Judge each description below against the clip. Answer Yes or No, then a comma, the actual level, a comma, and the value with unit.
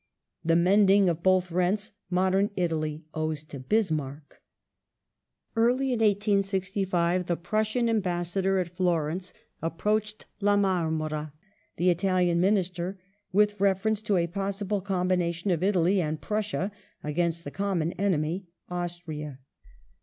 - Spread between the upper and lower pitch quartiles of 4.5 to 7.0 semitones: No, average, 3.0 semitones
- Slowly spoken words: Yes, slow, 115 wpm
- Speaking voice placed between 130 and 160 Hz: No, medium, 185 Hz